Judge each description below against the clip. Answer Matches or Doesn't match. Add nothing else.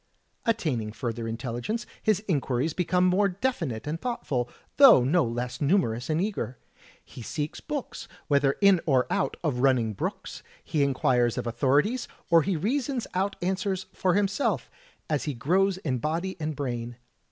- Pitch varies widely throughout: Matches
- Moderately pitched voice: Matches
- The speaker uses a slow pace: Doesn't match